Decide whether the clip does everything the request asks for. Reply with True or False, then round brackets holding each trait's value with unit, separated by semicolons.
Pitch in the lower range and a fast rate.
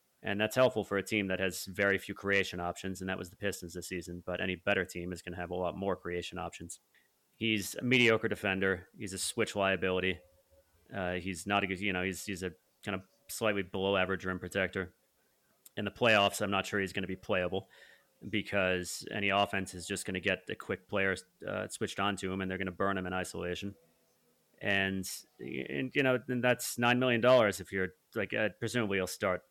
True (95 Hz; 220 wpm)